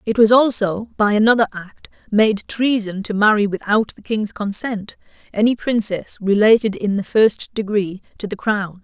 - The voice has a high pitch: Yes, high, 210 Hz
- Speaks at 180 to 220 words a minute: No, average, 165 wpm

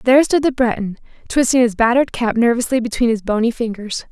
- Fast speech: No, average, 190 wpm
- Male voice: No, female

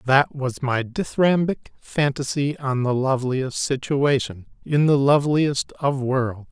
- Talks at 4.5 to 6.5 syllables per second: No, 4.1 syllables/s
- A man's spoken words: Yes, male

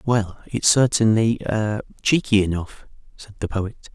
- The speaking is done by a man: Yes, male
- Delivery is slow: Yes, slow, 105 wpm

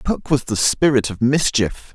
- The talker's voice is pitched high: No, low, 130 Hz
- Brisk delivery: No, average, 185 wpm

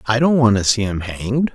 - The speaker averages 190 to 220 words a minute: No, fast, 270 wpm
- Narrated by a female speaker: No, male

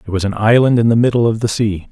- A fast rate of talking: Yes, fast, 315 wpm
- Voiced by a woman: No, male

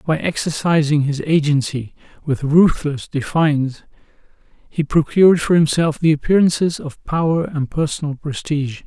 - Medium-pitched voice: Yes, medium, 150 Hz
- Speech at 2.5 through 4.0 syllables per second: No, 4.9 syllables/s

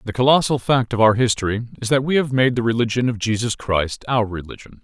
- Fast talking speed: Yes, fast, 225 wpm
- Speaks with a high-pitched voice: No, low, 120 Hz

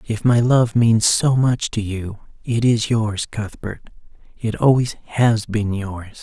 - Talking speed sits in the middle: Yes, average, 155 wpm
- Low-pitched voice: Yes, low, 110 Hz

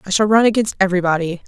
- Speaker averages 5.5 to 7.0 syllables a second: No, 7.6 syllables/s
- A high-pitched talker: Yes, high, 195 Hz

